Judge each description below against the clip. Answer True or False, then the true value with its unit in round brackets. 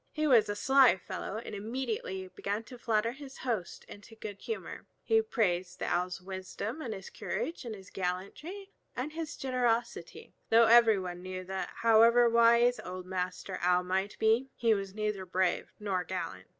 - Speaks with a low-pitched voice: False (215 Hz)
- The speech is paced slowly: False (165 wpm)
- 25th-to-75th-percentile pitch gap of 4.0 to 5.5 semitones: True (4.3 semitones)